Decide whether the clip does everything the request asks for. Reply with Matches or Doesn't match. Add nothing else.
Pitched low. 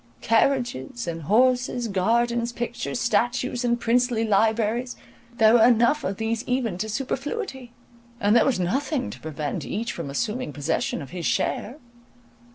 Doesn't match